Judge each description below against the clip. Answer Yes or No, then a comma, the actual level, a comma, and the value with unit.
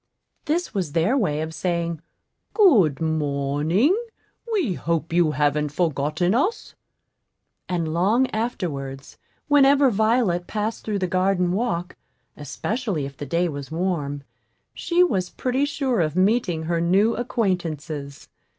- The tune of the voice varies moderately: No, wide, 6.5 semitones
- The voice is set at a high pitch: No, medium, 175 Hz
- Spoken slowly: Yes, slow, 125 wpm